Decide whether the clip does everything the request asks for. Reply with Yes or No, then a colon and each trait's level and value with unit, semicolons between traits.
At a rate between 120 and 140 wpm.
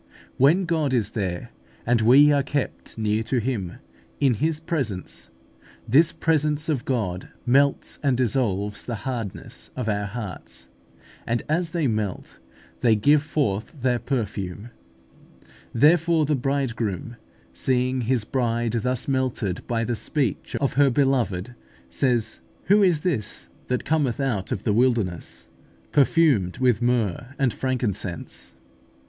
Yes: slow, 135 wpm